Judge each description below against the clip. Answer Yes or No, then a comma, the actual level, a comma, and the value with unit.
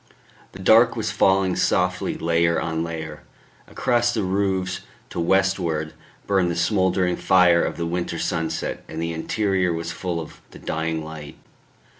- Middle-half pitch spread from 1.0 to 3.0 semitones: Yes, narrow, 2.5 semitones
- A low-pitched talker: Yes, very low, 85 Hz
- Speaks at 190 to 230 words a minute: No, average, 150 wpm